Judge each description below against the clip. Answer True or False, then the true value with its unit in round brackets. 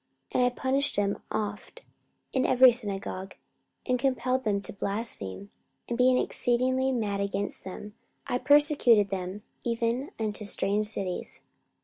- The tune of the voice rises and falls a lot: False (4.1 semitones)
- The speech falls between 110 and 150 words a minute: True (135 wpm)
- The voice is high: True (225 Hz)